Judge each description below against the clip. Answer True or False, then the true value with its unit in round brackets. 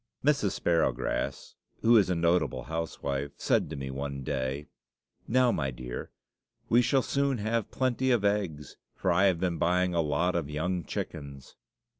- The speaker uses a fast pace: False (160 wpm)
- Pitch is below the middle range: True (85 Hz)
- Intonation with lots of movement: True (6.6 semitones)